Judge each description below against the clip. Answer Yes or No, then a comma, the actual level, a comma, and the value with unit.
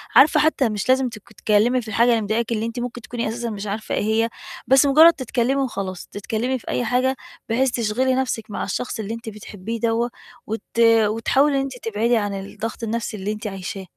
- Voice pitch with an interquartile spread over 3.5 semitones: No, average, 3.1 semitones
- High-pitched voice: Yes, high, 230 Hz